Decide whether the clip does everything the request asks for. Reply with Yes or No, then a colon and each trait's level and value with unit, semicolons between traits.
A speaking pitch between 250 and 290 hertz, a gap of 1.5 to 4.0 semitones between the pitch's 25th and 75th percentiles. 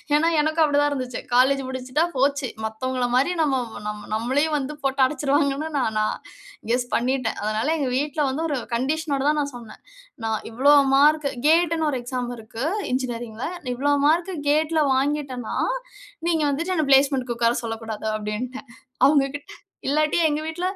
Yes: very high, 275 Hz; average, 3.4 semitones